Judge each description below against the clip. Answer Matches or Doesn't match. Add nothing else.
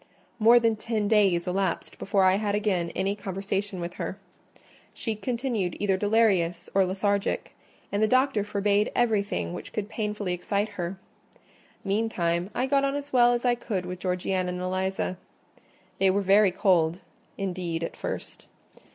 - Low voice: Doesn't match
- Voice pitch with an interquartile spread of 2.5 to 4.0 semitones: Matches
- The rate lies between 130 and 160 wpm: Matches